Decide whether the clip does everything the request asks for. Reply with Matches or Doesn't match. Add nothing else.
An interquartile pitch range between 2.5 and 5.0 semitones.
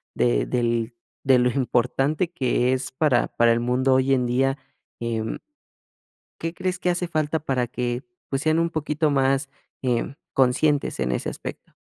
Matches